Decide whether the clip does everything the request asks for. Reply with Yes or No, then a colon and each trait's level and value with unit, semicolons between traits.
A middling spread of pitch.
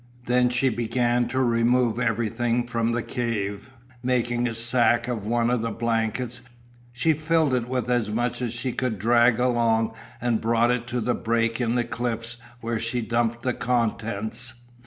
No: narrow, 1.2 semitones